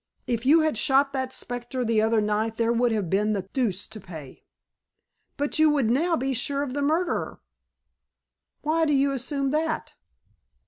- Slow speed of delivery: No, average, 175 wpm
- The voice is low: No, very high, 260 Hz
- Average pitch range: Yes, average, 4.4 semitones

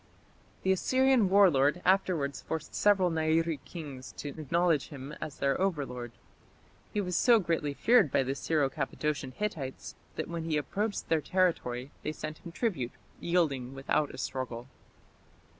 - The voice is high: No, medium, 155 Hz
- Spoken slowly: No, average, 150 wpm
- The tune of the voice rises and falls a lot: No, average, 4.9 semitones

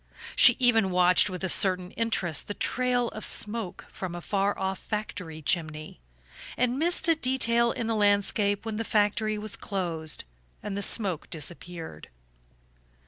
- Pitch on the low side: No, high, 205 Hz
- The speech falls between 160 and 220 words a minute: No, average, 150 wpm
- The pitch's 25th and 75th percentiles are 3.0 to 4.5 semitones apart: Yes, average, 4.1 semitones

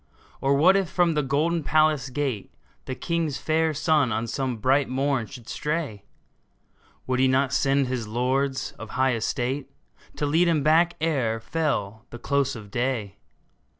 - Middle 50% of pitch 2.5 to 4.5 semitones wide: Yes, average, 3.7 semitones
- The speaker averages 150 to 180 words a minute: Yes, average, 160 wpm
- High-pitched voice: No, low, 135 Hz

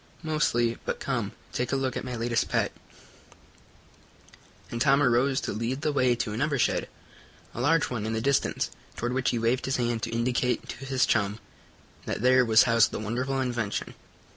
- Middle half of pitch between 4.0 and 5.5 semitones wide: No, narrow, 2.4 semitones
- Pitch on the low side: Yes, low, 125 Hz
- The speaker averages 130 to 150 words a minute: No, average, 185 wpm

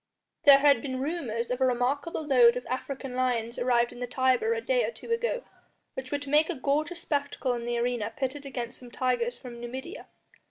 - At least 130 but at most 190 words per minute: No, fast, 205 wpm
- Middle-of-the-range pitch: No, very high, 260 Hz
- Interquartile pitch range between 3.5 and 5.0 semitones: No, average, 3.0 semitones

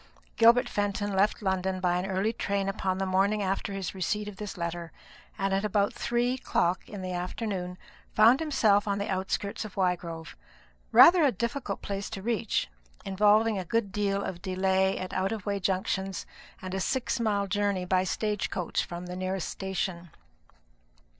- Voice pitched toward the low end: No, high, 195 Hz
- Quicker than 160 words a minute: Yes, average, 175 wpm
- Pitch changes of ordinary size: No, narrow, 2.1 semitones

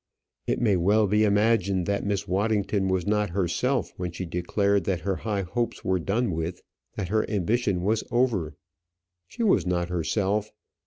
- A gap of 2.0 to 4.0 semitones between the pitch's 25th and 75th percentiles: Yes, average, 3.1 semitones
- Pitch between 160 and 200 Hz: No, low, 100 Hz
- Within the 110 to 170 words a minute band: Yes, average, 165 wpm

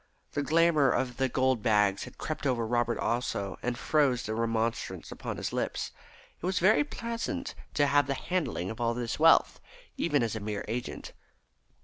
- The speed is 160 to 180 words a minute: Yes, average, 175 wpm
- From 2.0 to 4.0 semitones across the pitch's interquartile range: No, average, 4.6 semitones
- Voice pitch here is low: Yes, low, 125 Hz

